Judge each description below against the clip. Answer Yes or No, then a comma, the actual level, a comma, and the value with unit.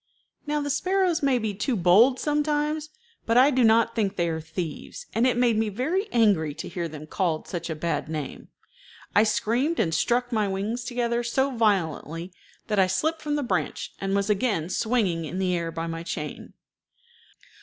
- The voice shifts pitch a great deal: Yes, wide, 6.8 semitones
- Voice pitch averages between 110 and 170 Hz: No, high, 215 Hz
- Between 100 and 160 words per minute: No, average, 185 wpm